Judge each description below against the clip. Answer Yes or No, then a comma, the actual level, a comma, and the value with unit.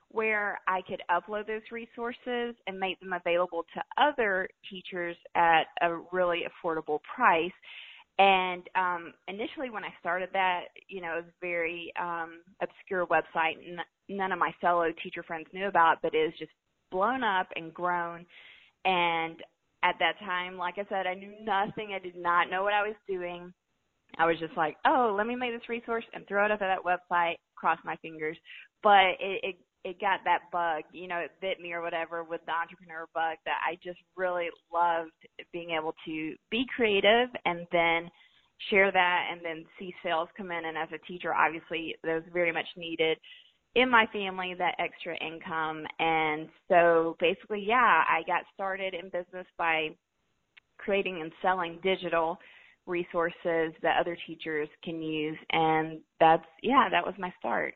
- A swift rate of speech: No, average, 175 wpm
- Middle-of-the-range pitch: Yes, medium, 175 Hz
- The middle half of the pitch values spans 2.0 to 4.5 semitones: Yes, narrow, 2.5 semitones